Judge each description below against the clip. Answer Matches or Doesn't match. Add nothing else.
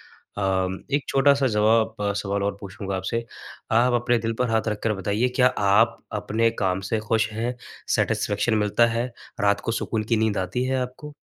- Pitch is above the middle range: Doesn't match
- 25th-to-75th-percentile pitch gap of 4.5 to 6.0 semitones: Doesn't match